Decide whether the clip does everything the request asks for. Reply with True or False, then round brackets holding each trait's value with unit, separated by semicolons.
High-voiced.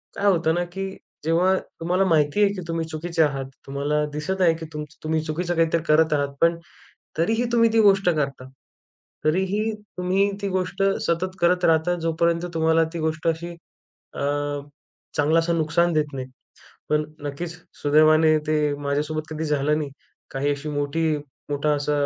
False (160 Hz)